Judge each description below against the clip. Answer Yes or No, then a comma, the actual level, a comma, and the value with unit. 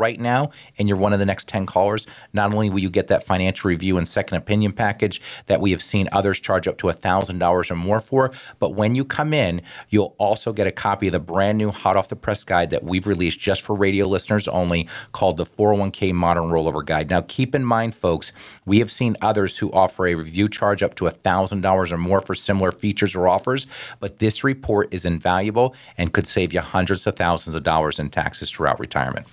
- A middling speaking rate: No, fast, 225 wpm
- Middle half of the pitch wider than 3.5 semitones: No, average, 2.9 semitones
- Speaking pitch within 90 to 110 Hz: Yes, low, 100 Hz